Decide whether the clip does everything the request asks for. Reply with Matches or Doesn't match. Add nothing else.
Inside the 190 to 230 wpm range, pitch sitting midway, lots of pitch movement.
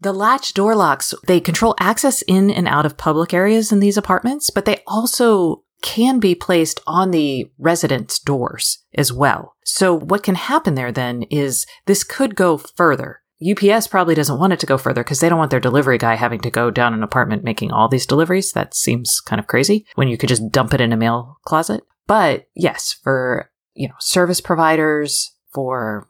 Matches